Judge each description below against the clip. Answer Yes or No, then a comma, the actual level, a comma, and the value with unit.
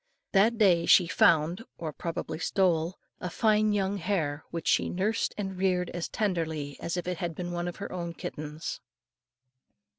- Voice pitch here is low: No, medium, 175 Hz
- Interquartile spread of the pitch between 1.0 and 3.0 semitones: Yes, average, 2.7 semitones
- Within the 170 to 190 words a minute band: Yes, average, 175 wpm